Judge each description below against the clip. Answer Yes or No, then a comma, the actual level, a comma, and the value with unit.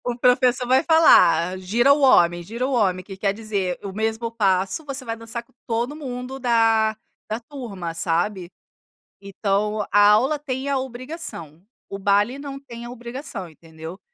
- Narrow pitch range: No, average, 4.7 semitones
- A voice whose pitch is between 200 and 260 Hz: Yes, high, 225 Hz